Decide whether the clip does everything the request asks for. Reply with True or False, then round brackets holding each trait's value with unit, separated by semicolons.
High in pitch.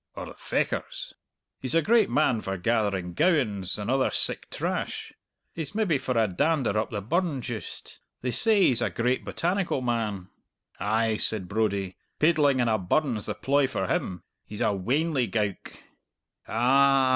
False (120 Hz)